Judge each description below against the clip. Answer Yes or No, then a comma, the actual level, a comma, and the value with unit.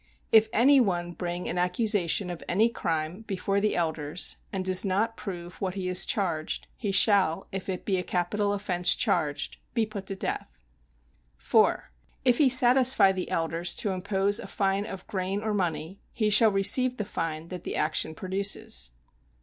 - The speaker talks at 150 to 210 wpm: Yes, average, 175 wpm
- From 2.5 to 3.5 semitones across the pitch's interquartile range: Yes, average, 3.0 semitones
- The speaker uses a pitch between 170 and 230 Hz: Yes, high, 190 Hz